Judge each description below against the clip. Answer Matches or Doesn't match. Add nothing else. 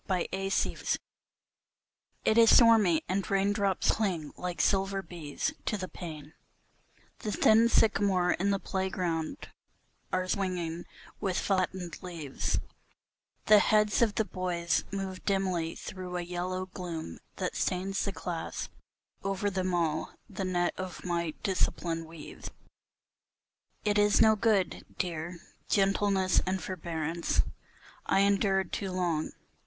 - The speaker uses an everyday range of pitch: Doesn't match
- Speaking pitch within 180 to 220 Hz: Matches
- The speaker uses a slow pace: Matches